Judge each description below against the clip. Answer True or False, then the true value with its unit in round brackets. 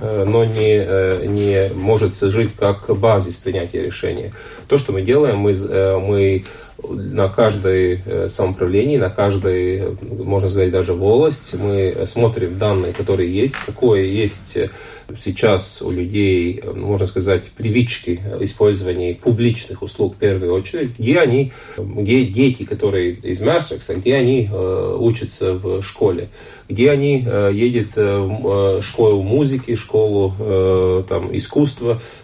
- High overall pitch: False (100 Hz)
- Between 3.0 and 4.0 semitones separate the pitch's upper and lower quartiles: True (3.3 semitones)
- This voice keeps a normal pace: True (120 wpm)